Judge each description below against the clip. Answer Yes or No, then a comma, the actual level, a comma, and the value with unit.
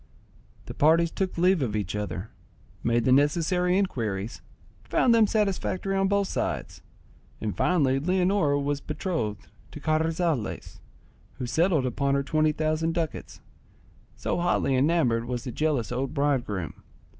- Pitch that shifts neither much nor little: No, wide, 5.8 semitones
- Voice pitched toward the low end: No, medium, 150 Hz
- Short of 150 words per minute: Yes, slow, 135 wpm